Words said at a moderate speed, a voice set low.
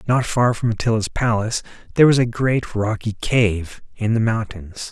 Yes: average, 170 wpm; low, 110 Hz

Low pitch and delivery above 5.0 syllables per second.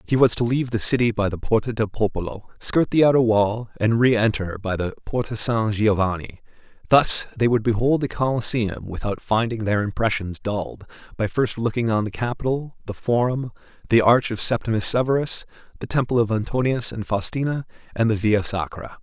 Yes: low, 115 Hz; 5.4 syllables/s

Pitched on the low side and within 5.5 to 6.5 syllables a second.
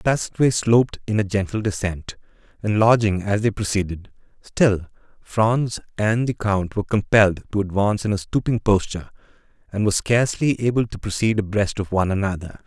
Yes: low, 105 Hz; 5.8 syllables/s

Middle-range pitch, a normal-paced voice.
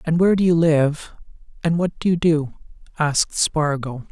Yes: medium, 160 Hz; average, 175 wpm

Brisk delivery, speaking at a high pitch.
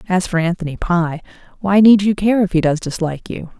No: fast, 215 wpm; medium, 180 Hz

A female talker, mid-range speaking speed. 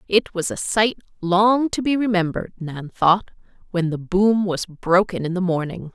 Yes: female; average, 180 wpm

